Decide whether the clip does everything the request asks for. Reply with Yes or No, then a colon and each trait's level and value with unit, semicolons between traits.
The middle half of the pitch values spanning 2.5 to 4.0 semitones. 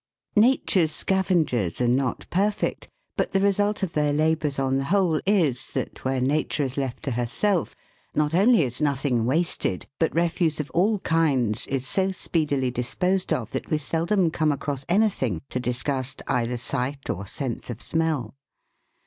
No: average, 5.2 semitones